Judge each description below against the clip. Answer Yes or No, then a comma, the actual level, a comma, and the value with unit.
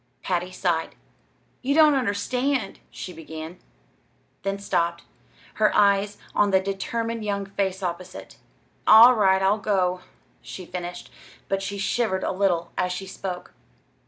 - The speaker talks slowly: Yes, slow, 130 wpm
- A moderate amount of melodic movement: No, narrow, 2.3 semitones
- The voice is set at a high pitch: Yes, high, 195 Hz